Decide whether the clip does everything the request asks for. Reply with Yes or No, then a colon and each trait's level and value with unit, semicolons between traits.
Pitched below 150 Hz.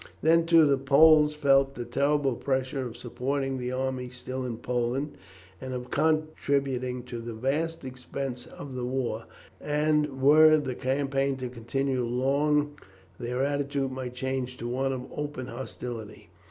Yes: low, 135 Hz